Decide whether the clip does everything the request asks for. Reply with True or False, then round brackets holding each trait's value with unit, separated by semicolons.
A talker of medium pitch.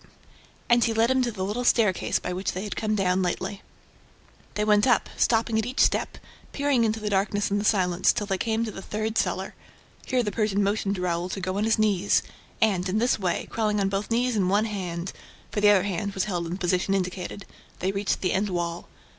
False (205 Hz)